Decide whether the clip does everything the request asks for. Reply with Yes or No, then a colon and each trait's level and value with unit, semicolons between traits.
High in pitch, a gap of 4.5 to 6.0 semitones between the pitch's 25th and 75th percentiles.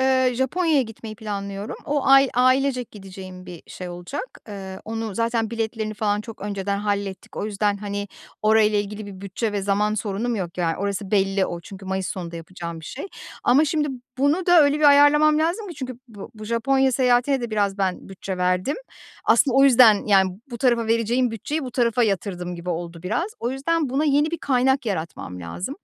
Yes: high, 215 Hz; average, 5.3 semitones